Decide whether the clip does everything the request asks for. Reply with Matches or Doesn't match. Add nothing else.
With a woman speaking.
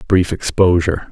Doesn't match